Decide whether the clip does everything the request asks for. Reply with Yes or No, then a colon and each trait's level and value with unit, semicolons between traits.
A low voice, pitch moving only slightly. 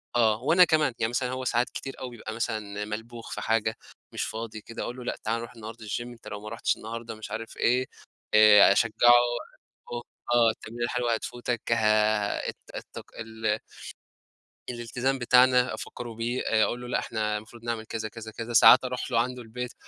Yes: low, 115 Hz; narrow, 1.9 semitones